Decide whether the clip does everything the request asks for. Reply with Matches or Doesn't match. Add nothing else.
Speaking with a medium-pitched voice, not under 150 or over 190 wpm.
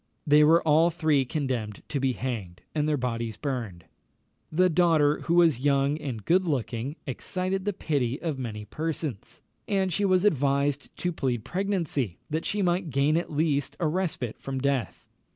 Matches